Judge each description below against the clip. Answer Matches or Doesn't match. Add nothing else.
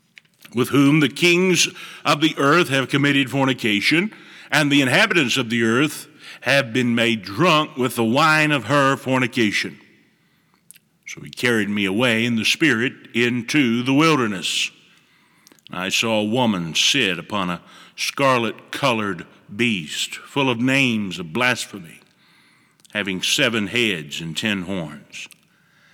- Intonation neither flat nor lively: Matches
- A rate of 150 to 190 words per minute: Doesn't match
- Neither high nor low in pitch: Doesn't match